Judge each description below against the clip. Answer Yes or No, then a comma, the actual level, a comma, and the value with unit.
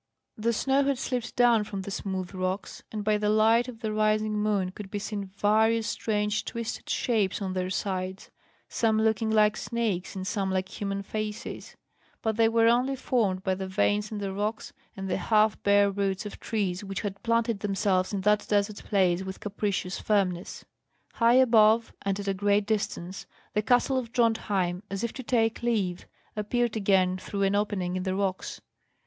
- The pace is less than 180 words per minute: No, average, 185 wpm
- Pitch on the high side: Yes, high, 210 Hz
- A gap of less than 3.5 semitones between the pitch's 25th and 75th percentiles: Yes, narrow, 2.5 semitones